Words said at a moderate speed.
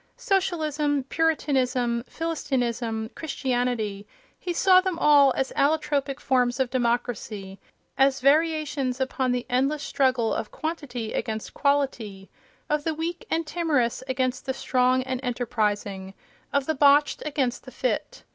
No: slow, 125 wpm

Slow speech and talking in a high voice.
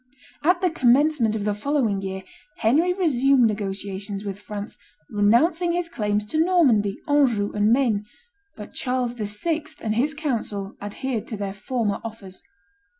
No: average, 145 wpm; high, 225 Hz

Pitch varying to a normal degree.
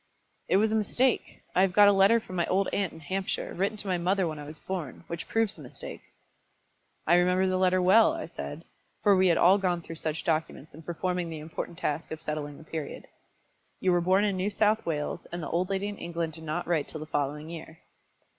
Yes: average, 3.3 semitones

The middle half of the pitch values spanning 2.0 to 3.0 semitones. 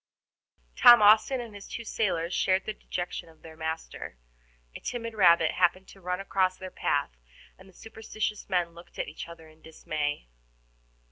No: average, 4.3 semitones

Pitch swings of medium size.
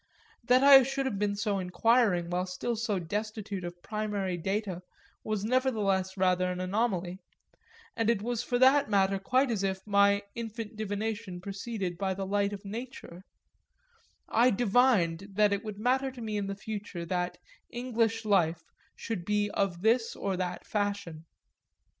Yes: average, 3.1 semitones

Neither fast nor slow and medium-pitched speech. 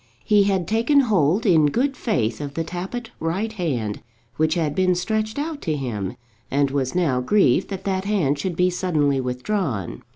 Yes: average, 175 wpm; medium, 175 Hz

